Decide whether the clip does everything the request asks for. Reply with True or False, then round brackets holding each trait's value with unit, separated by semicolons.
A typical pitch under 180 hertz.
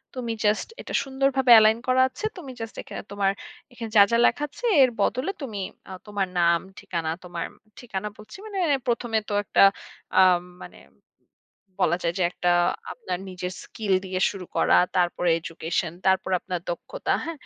False (210 Hz)